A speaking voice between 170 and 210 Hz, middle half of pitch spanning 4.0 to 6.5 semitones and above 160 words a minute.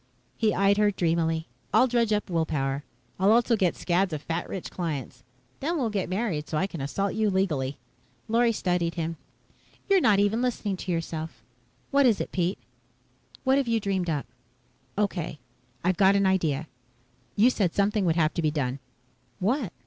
Yes: high, 190 Hz; average, 4.6 semitones; average, 180 wpm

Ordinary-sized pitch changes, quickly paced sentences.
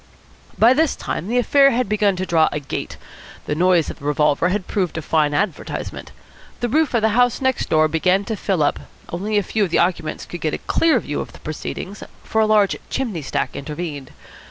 No: wide, 5.9 semitones; fast, 215 wpm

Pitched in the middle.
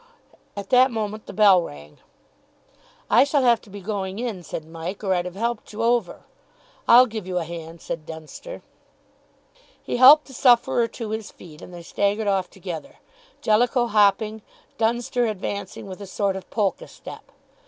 No: high, 205 Hz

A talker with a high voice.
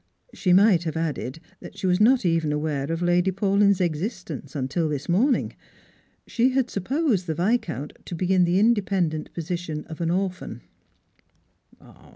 No: medium, 175 Hz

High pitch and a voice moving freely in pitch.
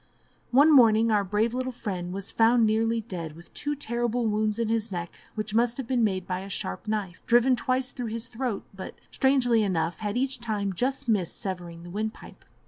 No: high, 220 Hz; average, 3.8 semitones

